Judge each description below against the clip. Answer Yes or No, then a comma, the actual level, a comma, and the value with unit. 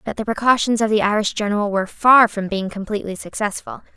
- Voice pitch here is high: Yes, high, 210 Hz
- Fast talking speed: No, average, 195 wpm